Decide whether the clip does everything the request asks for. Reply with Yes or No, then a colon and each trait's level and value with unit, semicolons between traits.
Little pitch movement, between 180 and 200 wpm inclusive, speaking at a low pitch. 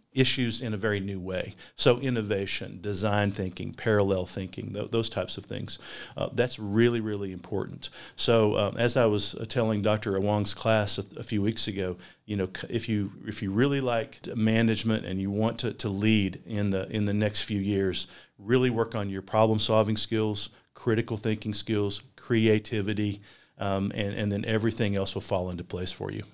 Yes: narrow, 2.2 semitones; average, 185 wpm; low, 105 Hz